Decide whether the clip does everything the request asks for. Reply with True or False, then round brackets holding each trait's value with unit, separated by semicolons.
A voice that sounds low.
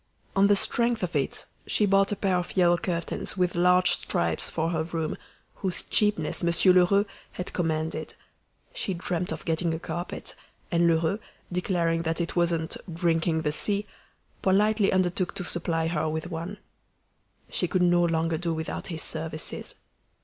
False (175 Hz)